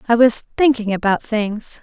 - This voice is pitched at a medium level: No, high, 225 Hz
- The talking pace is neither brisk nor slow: Yes, average, 165 wpm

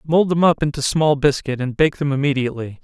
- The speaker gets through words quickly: Yes, fast, 210 wpm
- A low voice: No, medium, 145 Hz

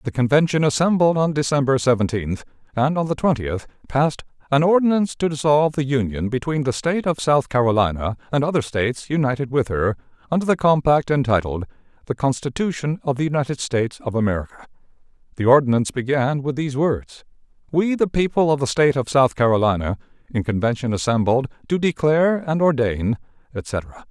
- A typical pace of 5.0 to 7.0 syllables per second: Yes, 6.0 syllables/s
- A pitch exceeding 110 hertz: Yes, low, 135 Hz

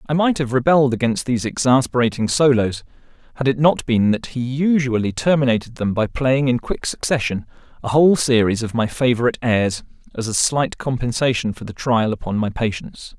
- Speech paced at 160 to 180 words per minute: Yes, average, 175 wpm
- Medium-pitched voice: No, low, 125 Hz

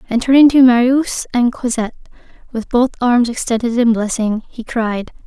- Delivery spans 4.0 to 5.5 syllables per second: Yes, 5.0 syllables/s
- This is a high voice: Yes, high, 240 Hz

